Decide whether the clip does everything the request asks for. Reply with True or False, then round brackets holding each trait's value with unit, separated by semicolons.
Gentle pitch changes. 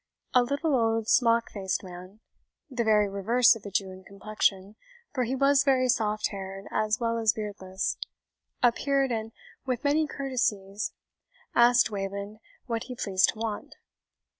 False (3.8 semitones)